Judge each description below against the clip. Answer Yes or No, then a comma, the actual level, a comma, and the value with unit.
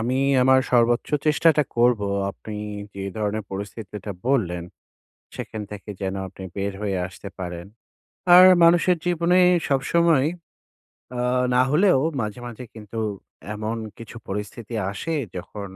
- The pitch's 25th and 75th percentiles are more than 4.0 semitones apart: Yes, average, 4.8 semitones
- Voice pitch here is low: Yes, low, 110 Hz